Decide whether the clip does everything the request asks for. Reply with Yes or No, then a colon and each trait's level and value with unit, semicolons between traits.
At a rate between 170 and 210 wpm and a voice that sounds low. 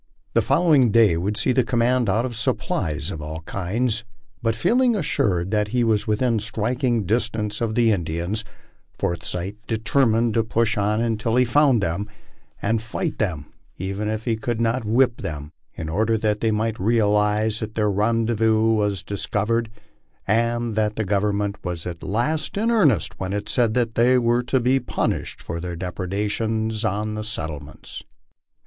Yes: average, 175 wpm; low, 110 Hz